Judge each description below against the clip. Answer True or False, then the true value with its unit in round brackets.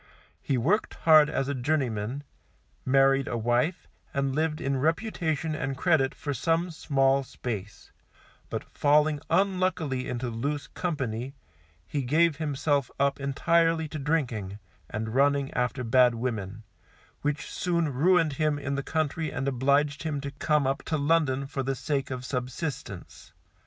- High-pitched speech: False (140 Hz)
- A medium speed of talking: True (145 wpm)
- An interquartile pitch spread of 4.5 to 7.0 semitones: False (3.3 semitones)